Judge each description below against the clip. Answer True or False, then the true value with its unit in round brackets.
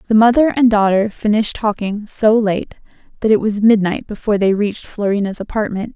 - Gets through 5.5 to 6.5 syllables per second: True (5.7 syllables/s)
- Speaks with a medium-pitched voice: False (210 Hz)